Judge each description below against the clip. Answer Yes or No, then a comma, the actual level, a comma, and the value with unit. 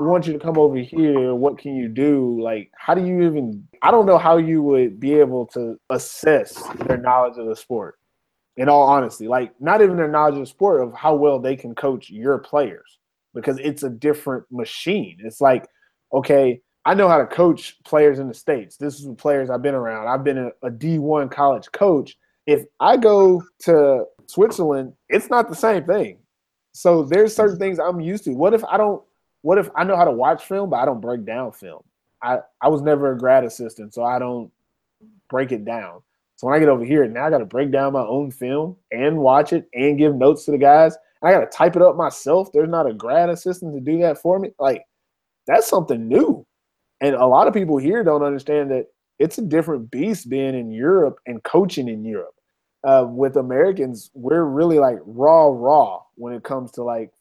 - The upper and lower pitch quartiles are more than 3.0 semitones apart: Yes, average, 4.6 semitones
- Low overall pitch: No, medium, 145 Hz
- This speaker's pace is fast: Yes, fast, 215 wpm